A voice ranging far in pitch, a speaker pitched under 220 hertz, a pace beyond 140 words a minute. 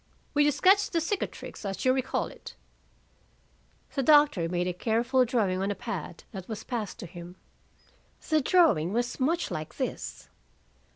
No: wide, 7.8 semitones; high, 240 Hz; average, 160 wpm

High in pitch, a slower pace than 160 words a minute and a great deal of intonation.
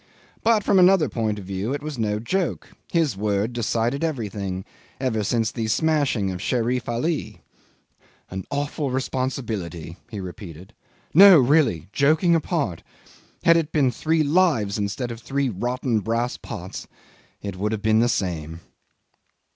No: low, 120 Hz; average, 145 wpm; wide, 6.2 semitones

